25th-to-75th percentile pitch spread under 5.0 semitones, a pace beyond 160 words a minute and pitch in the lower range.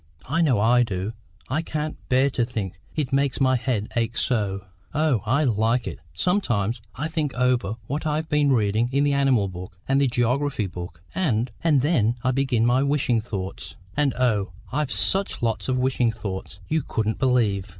Yes: average, 4.4 semitones; average, 180 wpm; low, 125 Hz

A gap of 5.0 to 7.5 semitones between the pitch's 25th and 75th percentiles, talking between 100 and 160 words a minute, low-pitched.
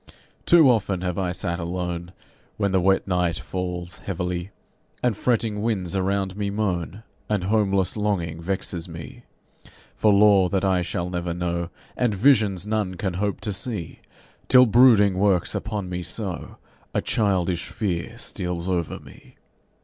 No: average, 2.9 semitones; average, 150 wpm; very low, 95 Hz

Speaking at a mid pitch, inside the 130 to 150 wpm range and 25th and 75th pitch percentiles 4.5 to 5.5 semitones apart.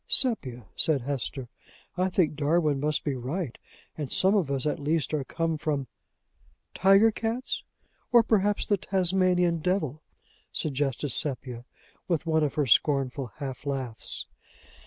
Yes: medium, 150 Hz; average, 140 wpm; average, 5.1 semitones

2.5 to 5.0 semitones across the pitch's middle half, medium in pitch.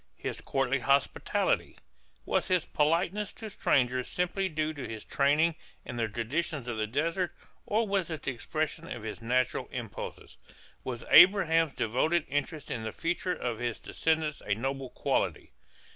No: wide, 5.4 semitones; medium, 150 Hz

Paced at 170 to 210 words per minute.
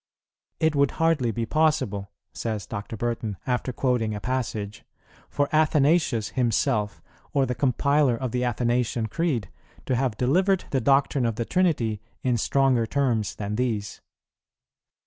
No: average, 140 wpm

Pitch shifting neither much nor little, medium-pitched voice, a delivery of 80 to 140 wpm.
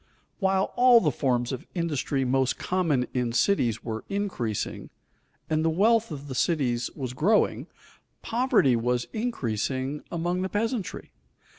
No: wide, 7.6 semitones; medium, 150 Hz; slow, 135 wpm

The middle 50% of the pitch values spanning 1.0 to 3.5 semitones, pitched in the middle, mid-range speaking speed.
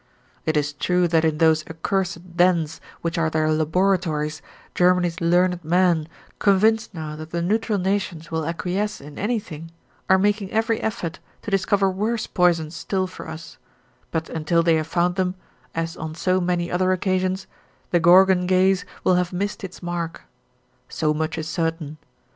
Yes: average, 2.7 semitones; medium, 175 Hz; average, 160 wpm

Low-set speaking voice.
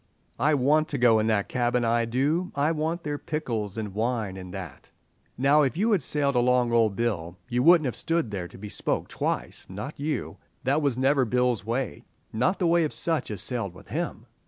Yes: low, 125 Hz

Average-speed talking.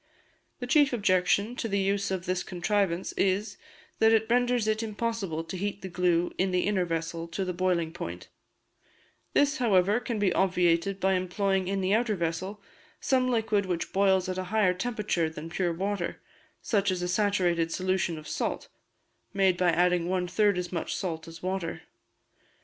Yes: average, 175 wpm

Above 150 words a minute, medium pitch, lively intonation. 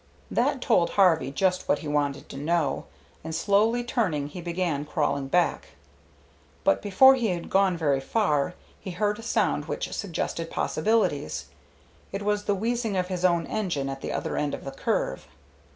Yes: average, 170 wpm; medium, 180 Hz; wide, 5.8 semitones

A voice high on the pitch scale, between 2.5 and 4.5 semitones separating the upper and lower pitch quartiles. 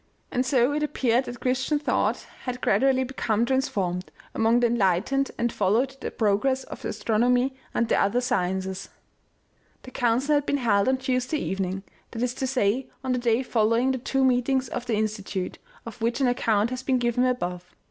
Yes: high, 245 Hz; average, 3.3 semitones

